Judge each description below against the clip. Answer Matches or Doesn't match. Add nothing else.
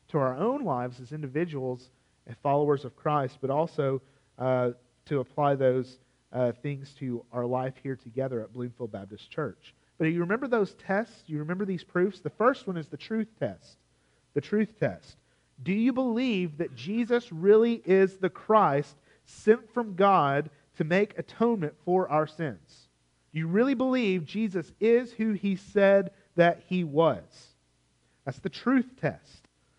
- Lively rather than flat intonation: Matches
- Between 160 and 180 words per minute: Matches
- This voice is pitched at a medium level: Matches